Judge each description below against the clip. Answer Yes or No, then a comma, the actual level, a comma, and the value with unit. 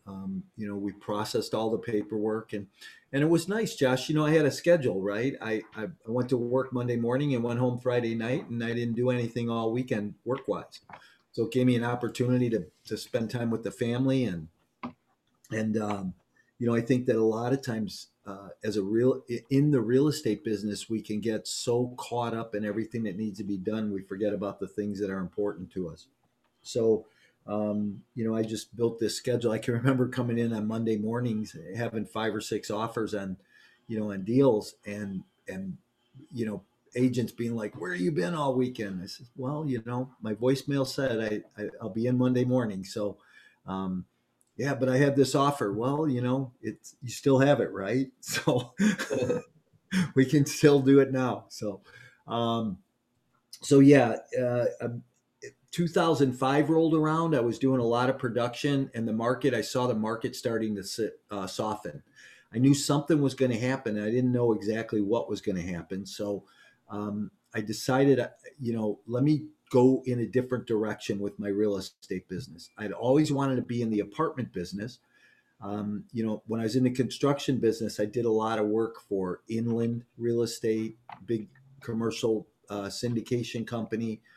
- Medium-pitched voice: No, low, 115 Hz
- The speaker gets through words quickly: No, average, 195 wpm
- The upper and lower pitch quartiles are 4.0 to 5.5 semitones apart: No, average, 3.3 semitones